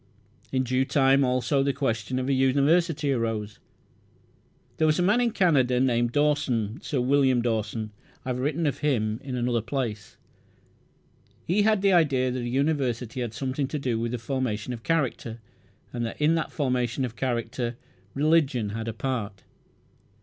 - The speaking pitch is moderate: No, low, 130 Hz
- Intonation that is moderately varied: Yes, average, 3.5 semitones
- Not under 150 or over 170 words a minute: Yes, average, 165 wpm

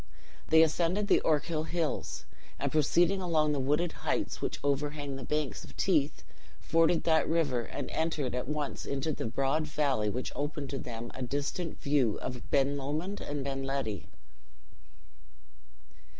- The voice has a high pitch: No, medium, 145 Hz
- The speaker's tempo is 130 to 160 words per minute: Yes, average, 150 wpm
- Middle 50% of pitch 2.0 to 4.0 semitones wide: Yes, average, 2.9 semitones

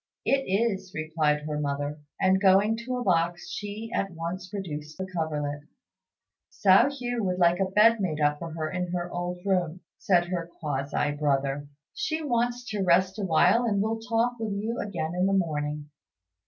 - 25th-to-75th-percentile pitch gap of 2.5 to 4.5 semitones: No, average, 5.1 semitones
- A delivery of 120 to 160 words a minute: No, average, 175 wpm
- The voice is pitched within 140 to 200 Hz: Yes, medium, 185 Hz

